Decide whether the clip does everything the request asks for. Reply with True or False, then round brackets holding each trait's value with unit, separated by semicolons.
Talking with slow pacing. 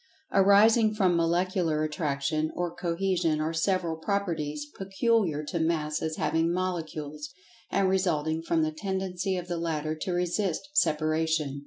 True (130 wpm)